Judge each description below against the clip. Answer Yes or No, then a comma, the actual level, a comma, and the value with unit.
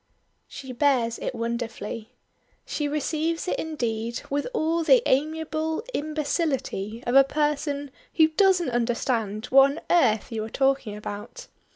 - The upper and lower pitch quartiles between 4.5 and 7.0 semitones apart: Yes, average, 5.2 semitones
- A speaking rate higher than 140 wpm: No, slow, 135 wpm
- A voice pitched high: Yes, very high, 275 Hz